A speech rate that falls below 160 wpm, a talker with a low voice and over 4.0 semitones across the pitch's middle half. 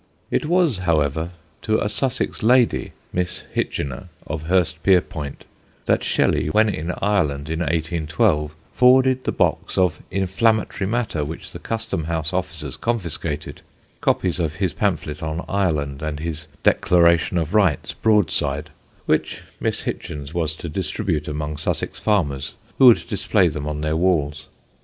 Yes: average, 140 wpm; very low, 85 Hz; average, 4.7 semitones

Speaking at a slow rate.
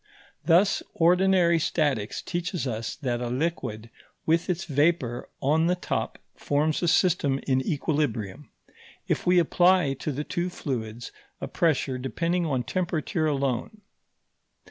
Yes: slow, 130 wpm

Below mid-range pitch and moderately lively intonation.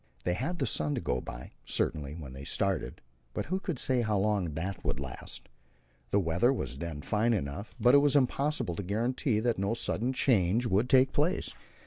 No: low, 105 Hz; wide, 6.9 semitones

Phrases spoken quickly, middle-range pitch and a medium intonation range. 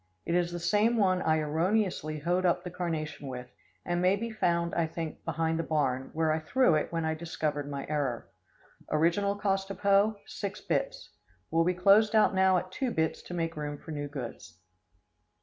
No: average, 195 wpm; medium, 170 Hz; average, 3.8 semitones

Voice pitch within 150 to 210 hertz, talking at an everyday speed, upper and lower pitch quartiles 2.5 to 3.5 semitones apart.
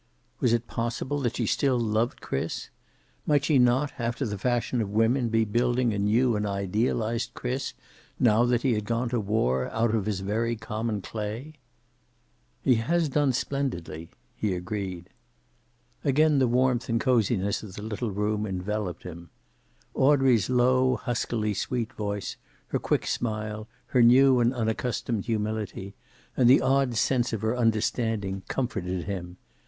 No: low, 115 Hz; average, 150 wpm; average, 3.1 semitones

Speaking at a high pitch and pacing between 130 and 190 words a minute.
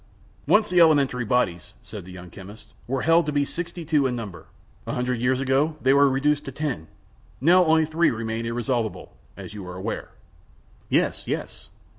No: low, 130 Hz; average, 180 wpm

